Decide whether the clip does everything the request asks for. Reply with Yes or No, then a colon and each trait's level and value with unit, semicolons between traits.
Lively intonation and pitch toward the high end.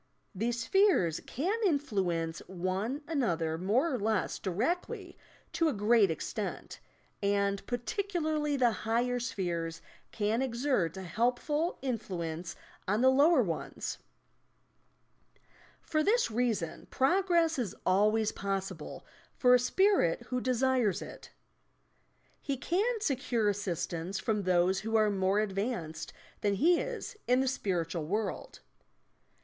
Yes: wide, 6.2 semitones; high, 225 Hz